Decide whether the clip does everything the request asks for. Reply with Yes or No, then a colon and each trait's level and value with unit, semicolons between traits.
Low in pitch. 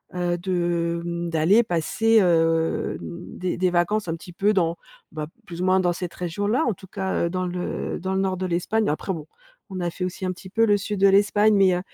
No: medium, 180 Hz